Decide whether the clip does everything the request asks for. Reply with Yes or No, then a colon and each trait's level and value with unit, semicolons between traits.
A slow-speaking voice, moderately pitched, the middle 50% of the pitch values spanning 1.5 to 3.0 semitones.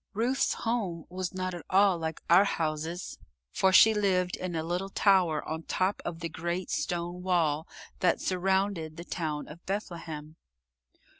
No: average, 155 wpm; medium, 175 Hz; average, 2.7 semitones